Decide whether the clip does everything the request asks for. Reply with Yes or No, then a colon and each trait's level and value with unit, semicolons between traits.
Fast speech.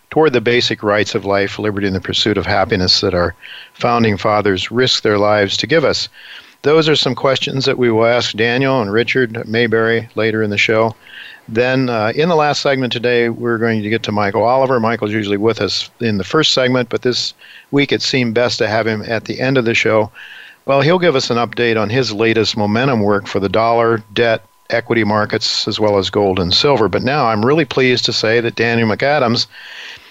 Yes: fast, 215 wpm